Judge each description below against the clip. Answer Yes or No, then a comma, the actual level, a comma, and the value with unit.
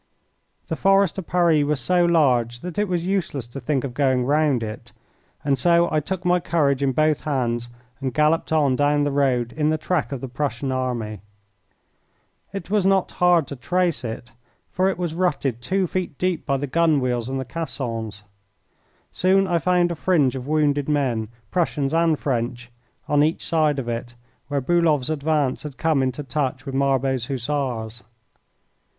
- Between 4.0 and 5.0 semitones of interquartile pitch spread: Yes, average, 4.6 semitones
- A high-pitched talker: No, medium, 145 Hz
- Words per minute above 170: Yes, average, 180 wpm